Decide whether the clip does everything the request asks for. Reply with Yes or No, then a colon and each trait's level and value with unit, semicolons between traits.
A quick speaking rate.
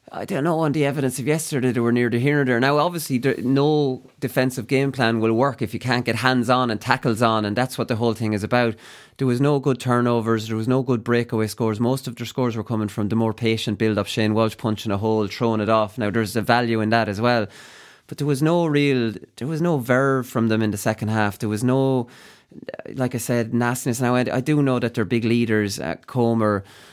Yes: fast, 250 wpm